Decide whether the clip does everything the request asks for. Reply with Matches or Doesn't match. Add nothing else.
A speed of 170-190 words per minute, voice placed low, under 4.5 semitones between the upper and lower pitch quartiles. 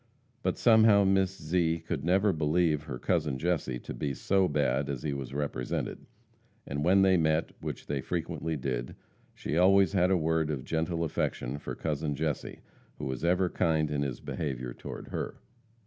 Matches